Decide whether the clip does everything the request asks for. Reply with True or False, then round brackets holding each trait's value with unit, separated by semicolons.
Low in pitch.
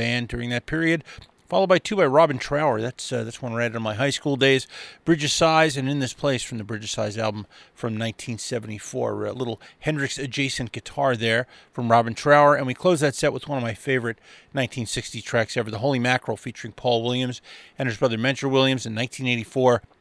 True (125 Hz)